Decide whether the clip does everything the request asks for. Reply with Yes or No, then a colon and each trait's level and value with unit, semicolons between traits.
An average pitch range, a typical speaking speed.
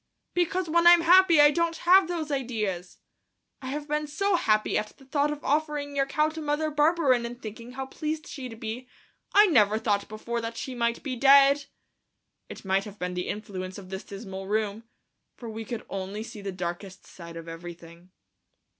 No: wide, 6.7 semitones; average, 190 wpm